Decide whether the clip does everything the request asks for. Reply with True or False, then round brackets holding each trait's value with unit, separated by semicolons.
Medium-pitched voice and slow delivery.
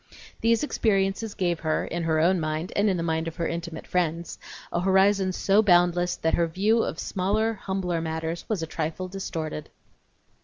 False (175 Hz; 180 wpm)